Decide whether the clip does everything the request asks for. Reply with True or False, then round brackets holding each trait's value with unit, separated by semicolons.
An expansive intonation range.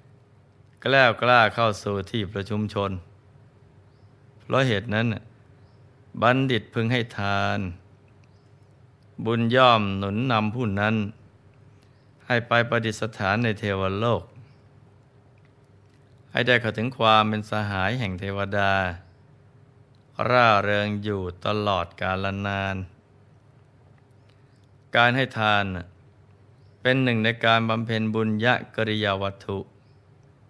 False (3.8 semitones)